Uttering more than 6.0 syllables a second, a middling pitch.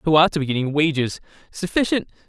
Yes: 6.4 syllables/s; medium, 160 Hz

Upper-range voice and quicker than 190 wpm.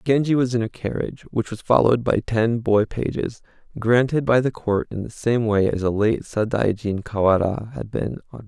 No: low, 115 Hz; average, 200 wpm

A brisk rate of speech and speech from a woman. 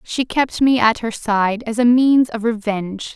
Yes: fast, 210 wpm; female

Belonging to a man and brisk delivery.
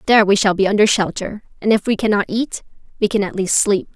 No: female; fast, 245 wpm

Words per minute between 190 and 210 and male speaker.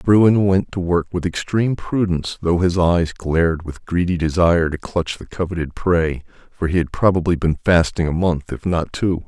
Yes: average, 195 wpm; male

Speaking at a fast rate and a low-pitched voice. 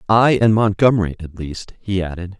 No: average, 175 wpm; low, 100 Hz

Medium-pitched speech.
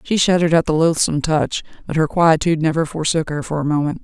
Yes: medium, 160 Hz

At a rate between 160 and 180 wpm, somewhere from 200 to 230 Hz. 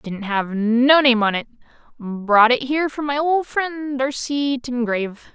No: average, 170 wpm; very high, 255 Hz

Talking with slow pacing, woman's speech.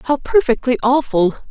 Yes: slow, 120 wpm; female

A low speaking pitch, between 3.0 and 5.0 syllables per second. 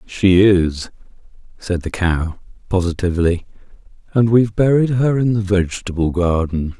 Yes: very low, 95 Hz; 4.7 syllables/s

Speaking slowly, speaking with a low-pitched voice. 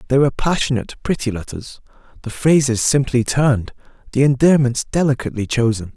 Yes: slow, 120 wpm; low, 130 Hz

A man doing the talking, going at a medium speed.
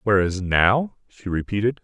No: male; slow, 130 wpm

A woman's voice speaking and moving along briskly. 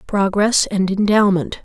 No: female; slow, 110 wpm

